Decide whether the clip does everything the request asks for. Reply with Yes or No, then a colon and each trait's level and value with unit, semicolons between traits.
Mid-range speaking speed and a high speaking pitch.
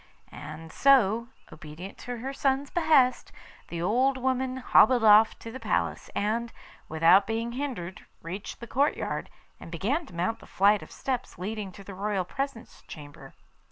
Yes: average, 155 wpm; high, 220 Hz